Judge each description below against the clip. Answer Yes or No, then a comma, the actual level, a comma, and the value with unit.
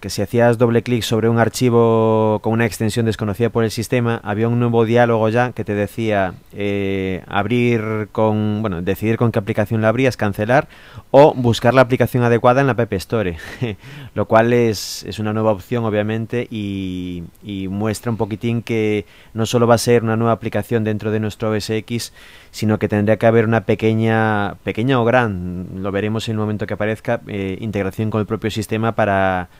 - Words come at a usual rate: Yes, average, 185 wpm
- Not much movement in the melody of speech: Yes, narrow, 2.0 semitones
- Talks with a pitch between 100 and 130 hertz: Yes, low, 110 Hz